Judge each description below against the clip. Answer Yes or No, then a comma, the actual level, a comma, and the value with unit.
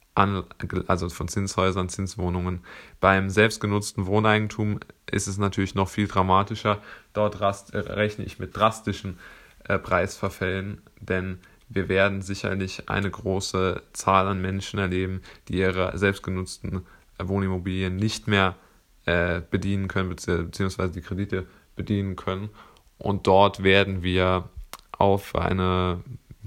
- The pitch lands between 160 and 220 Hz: No, very low, 95 Hz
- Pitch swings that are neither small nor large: No, narrow, 1.3 semitones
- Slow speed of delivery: Yes, slow, 120 wpm